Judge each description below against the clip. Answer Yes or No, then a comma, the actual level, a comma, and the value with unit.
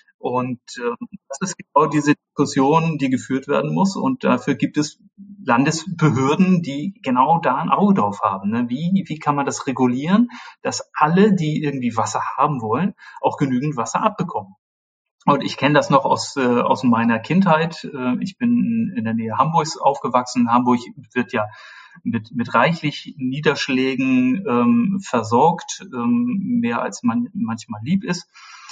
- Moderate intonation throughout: No, wide, 8.3 semitones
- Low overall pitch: No, medium, 155 Hz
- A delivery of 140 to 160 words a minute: Yes, average, 155 wpm